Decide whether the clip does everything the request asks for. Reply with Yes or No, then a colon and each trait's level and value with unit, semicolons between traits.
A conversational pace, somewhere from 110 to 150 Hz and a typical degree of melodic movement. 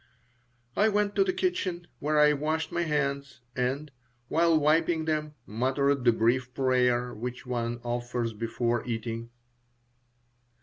No: slow, 130 wpm; low, 135 Hz; average, 4.5 semitones